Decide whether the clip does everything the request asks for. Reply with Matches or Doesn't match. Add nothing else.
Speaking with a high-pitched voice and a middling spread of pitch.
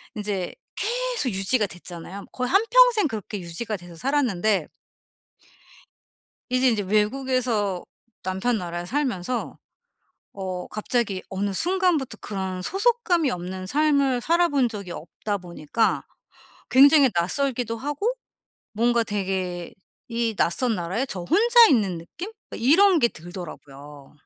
Doesn't match